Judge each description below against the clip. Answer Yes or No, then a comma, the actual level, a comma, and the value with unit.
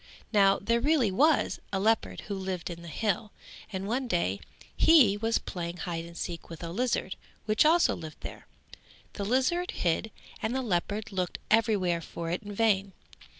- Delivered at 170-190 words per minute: Yes, average, 180 wpm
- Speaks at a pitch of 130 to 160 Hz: No, high, 200 Hz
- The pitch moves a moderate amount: Yes, average, 4.6 semitones